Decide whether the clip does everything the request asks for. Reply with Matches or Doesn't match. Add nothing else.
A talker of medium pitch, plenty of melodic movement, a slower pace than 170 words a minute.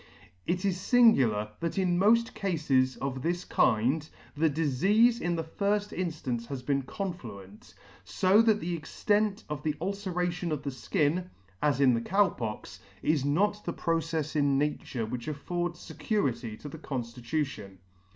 Matches